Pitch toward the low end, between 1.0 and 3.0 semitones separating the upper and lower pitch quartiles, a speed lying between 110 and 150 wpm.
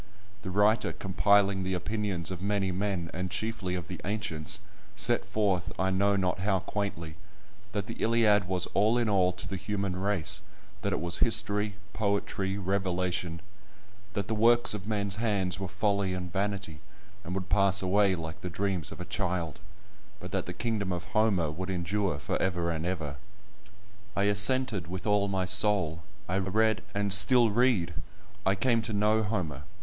No: very low, 95 Hz; narrow, 2.4 semitones; average, 170 wpm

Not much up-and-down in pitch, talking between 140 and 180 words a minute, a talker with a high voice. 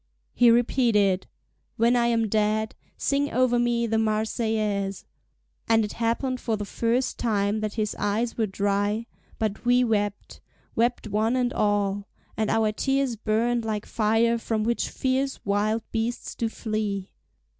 Yes: narrow, 2.1 semitones; average, 145 wpm; high, 220 Hz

